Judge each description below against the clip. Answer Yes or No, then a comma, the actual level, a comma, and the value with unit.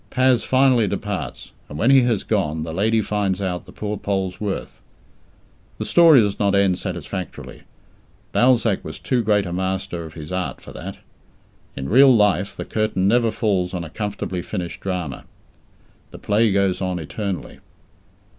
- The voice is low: Yes, low, 100 Hz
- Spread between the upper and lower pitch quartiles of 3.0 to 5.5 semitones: Yes, average, 3.3 semitones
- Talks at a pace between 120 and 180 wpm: Yes, average, 165 wpm